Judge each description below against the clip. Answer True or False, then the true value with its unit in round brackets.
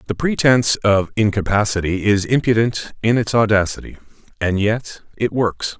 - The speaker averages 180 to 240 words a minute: False (135 wpm)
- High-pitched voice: False (105 Hz)